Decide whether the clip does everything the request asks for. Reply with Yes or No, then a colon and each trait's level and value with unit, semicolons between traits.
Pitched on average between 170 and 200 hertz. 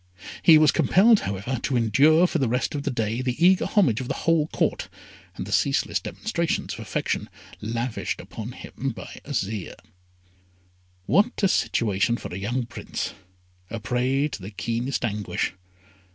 No: low, 125 Hz